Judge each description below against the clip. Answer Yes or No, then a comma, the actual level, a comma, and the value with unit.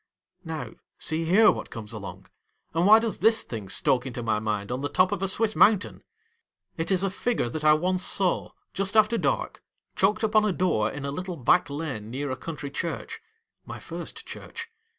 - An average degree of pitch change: No, wide, 7.4 semitones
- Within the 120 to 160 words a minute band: No, average, 200 wpm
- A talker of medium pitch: Yes, medium, 165 Hz